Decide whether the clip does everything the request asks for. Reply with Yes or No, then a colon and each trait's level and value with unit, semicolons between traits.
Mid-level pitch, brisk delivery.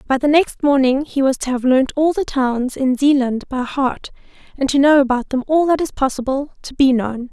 No: very high, 270 Hz; fast, 230 wpm